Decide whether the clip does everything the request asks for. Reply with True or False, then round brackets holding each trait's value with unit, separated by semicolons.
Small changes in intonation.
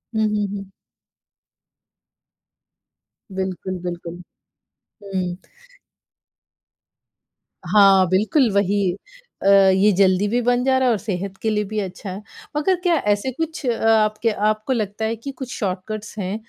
False (3.4 semitones)